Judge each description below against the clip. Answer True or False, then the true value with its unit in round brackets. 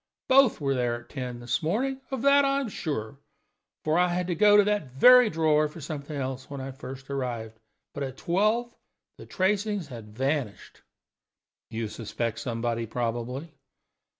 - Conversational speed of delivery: True (165 wpm)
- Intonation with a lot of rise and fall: True (8.3 semitones)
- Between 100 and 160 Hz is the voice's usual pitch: True (140 Hz)